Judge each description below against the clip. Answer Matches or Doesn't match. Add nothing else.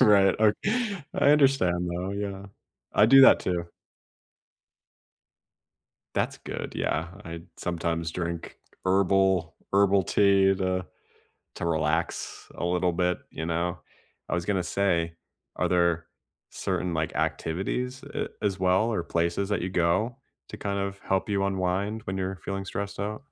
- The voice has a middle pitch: Doesn't match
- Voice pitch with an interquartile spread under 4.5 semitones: Matches